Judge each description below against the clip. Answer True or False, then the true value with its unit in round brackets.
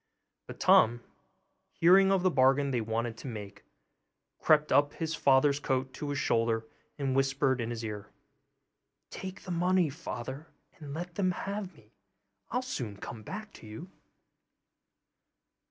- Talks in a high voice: False (140 Hz)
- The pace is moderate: True (145 wpm)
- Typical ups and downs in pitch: False (6.8 semitones)